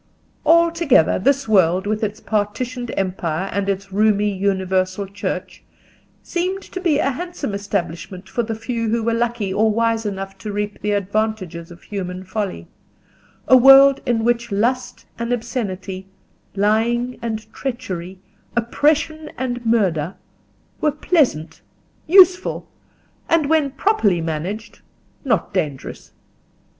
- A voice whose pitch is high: Yes, high, 215 Hz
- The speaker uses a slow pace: Yes, slow, 125 wpm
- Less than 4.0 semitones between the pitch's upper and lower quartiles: No, average, 4.7 semitones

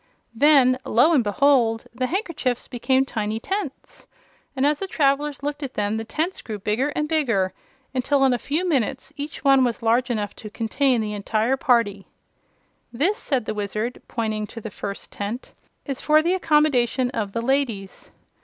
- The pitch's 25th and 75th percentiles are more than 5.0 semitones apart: No, average, 4.5 semitones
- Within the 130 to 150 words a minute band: No, average, 175 wpm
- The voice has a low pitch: No, very high, 255 Hz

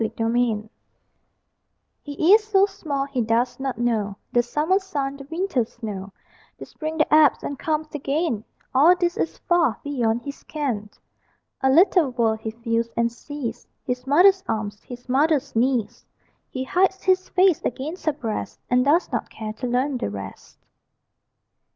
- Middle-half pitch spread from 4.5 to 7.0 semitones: Yes, average, 5.2 semitones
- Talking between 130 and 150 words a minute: No, average, 165 wpm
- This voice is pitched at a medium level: No, very high, 265 Hz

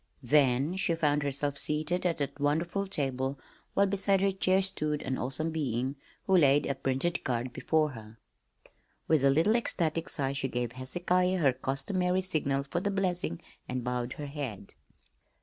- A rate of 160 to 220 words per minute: Yes, average, 165 wpm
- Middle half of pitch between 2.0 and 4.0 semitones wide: No, average, 5.0 semitones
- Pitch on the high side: No, medium, 145 Hz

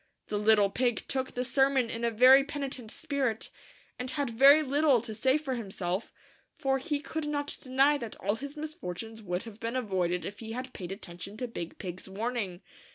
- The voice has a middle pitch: No, high, 240 Hz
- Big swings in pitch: No, average, 4.7 semitones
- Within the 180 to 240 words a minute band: Yes, average, 200 wpm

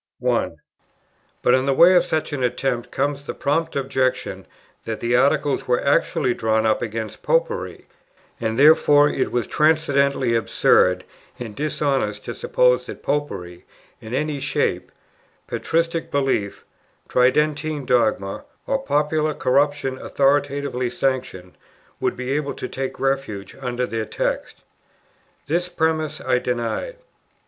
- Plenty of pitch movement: No, average, 3.7 semitones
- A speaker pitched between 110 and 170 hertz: Yes, low, 135 Hz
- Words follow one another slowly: Yes, slow, 130 wpm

